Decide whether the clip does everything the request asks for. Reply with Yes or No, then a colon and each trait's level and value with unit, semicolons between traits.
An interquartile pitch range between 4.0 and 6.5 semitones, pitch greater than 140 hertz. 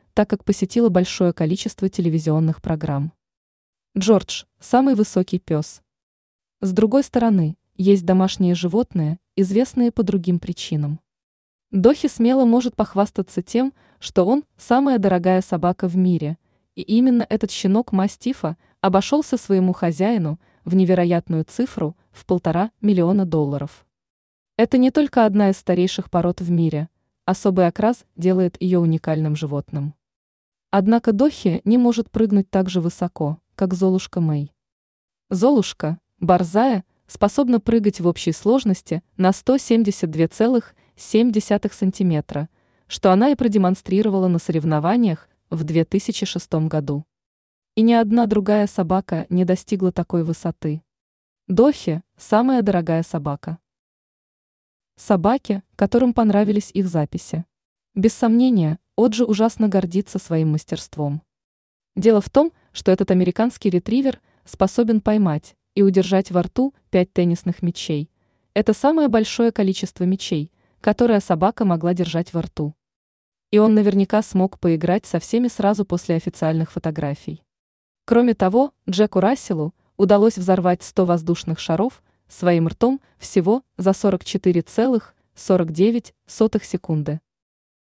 Yes: average, 4.4 semitones; high, 190 Hz